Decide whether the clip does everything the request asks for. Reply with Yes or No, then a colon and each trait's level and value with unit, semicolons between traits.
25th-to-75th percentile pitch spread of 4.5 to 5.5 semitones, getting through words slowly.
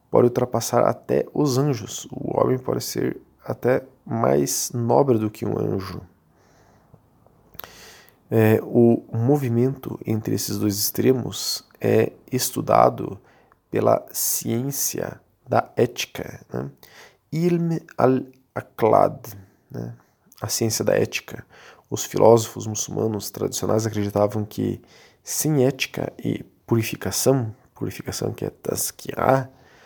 No: average, 3.7 semitones; slow, 100 wpm